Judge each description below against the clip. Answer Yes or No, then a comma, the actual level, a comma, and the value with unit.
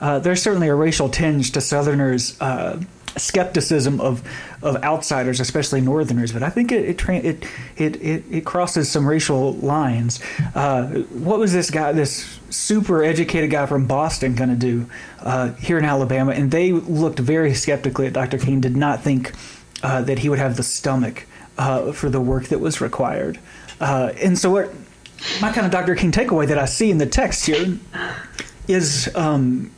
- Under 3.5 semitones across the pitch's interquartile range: No, average, 4.1 semitones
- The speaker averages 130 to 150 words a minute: No, average, 180 wpm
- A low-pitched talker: No, medium, 145 Hz